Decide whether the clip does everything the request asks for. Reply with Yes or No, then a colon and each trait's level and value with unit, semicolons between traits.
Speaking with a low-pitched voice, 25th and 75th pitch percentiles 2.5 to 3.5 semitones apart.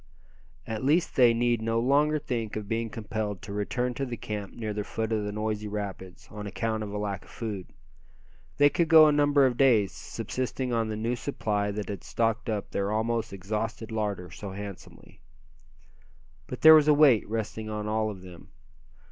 Yes: low, 110 Hz; average, 2.8 semitones